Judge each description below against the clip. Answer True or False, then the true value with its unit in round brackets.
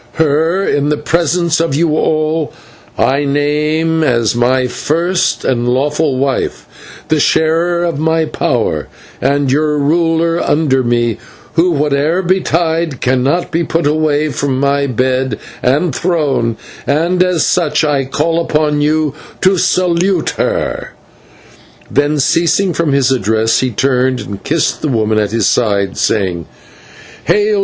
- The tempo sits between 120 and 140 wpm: True (135 wpm)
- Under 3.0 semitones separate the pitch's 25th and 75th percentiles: False (4.0 semitones)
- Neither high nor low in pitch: True (150 Hz)